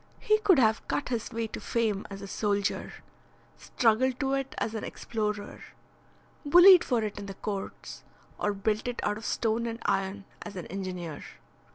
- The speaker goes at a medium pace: Yes, average, 175 wpm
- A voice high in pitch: Yes, high, 220 Hz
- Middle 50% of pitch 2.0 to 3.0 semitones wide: No, average, 3.5 semitones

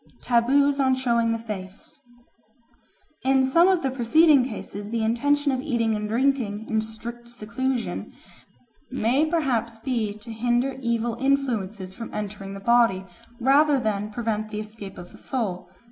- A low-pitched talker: No, high, 235 Hz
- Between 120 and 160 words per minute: Yes, average, 150 wpm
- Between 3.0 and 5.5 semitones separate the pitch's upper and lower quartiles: Yes, average, 3.6 semitones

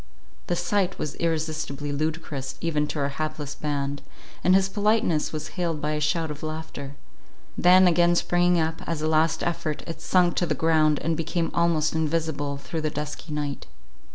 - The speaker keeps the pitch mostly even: Yes, narrow, 2.3 semitones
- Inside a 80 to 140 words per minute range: No, average, 170 wpm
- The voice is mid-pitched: Yes, medium, 160 Hz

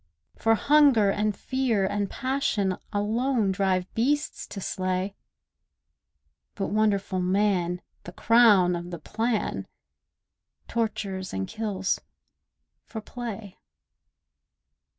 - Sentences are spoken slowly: Yes, slow, 95 wpm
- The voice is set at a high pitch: Yes, high, 205 Hz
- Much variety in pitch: No, average, 3.3 semitones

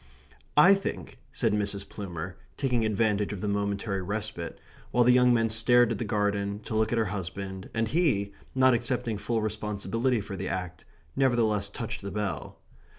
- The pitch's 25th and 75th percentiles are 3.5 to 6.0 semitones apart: No, average, 2.8 semitones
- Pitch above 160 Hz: No, low, 105 Hz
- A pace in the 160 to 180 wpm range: Yes, average, 170 wpm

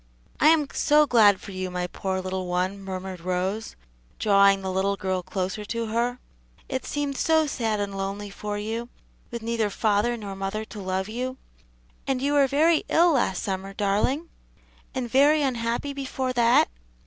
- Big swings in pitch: No, average, 5.0 semitones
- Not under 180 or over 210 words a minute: No, average, 170 wpm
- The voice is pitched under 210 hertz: No, high, 215 Hz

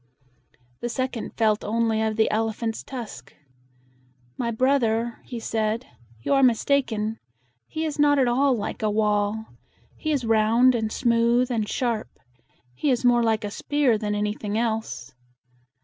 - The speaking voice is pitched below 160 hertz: No, high, 230 Hz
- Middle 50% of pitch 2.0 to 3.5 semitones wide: Yes, narrow, 2.6 semitones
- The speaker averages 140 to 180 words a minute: Yes, average, 150 wpm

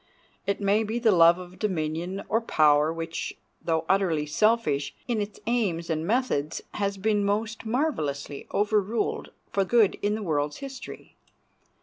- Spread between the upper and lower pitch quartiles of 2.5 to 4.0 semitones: No, average, 5.2 semitones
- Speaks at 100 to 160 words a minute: Yes, average, 145 wpm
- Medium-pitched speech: No, high, 195 Hz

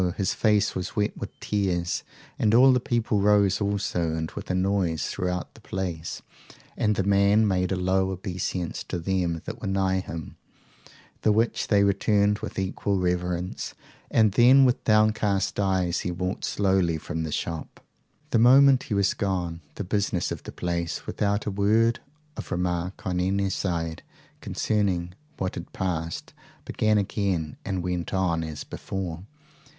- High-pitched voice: No, very low, 95 Hz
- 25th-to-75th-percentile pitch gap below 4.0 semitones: Yes, average, 2.7 semitones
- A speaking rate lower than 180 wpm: Yes, average, 160 wpm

